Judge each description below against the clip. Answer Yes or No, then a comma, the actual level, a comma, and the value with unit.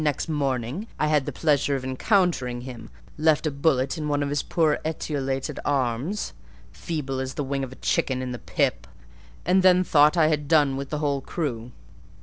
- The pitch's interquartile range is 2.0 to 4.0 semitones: Yes, average, 3.0 semitones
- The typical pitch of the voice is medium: Yes, medium, 145 Hz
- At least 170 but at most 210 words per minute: Yes, average, 190 wpm